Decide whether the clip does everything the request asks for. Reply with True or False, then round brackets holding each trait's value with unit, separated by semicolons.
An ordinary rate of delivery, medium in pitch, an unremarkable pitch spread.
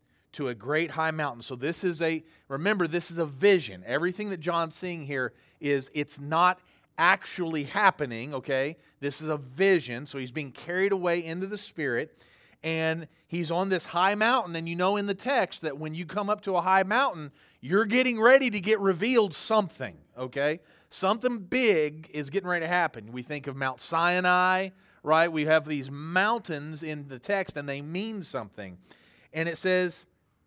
True (185 wpm; 165 Hz; 4.8 semitones)